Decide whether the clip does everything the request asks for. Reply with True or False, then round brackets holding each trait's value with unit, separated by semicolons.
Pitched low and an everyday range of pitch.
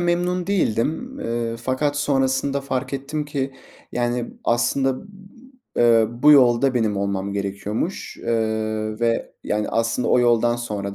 True (120 Hz; 3.8 semitones)